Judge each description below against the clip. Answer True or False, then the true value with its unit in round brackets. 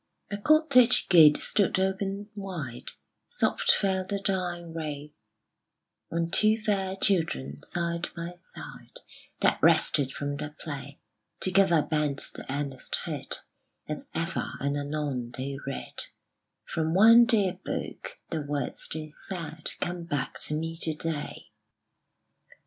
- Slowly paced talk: True (125 wpm)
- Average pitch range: True (4.7 semitones)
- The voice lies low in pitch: False (165 Hz)